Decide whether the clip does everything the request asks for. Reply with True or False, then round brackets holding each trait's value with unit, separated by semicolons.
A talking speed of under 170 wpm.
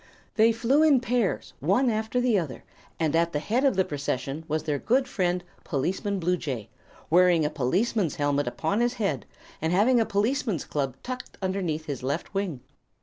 False (175 wpm)